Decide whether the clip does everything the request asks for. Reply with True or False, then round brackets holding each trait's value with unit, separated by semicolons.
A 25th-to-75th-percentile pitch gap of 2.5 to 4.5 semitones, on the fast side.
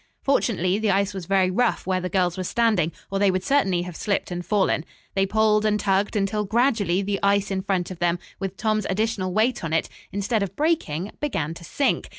True (2.8 semitones; 210 wpm)